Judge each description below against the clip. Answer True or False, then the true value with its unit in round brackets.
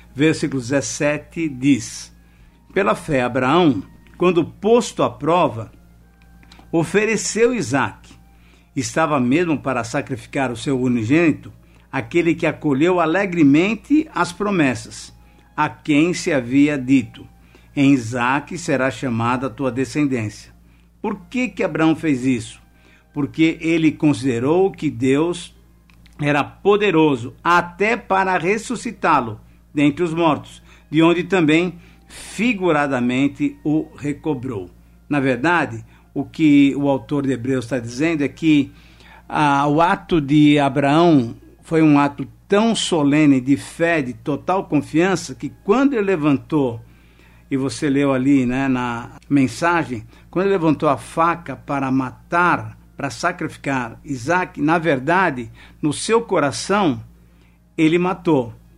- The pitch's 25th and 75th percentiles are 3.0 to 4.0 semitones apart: False (4.8 semitones)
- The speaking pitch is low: False (145 Hz)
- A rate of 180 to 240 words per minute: False (120 wpm)